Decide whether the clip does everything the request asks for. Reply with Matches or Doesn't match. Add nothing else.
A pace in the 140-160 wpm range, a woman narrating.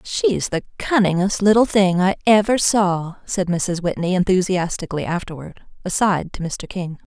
Matches